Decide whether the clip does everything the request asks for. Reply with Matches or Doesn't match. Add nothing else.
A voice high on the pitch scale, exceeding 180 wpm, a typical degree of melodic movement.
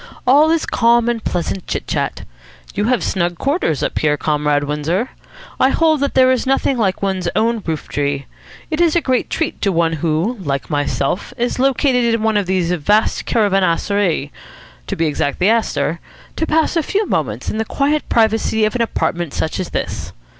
Doesn't match